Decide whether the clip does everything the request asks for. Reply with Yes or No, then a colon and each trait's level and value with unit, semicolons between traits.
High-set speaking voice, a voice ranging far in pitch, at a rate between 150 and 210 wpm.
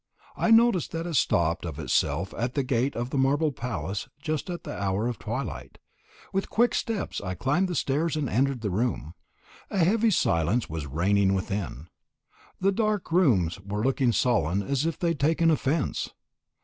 No: low, 130 Hz; wide, 8.9 semitones; average, 175 wpm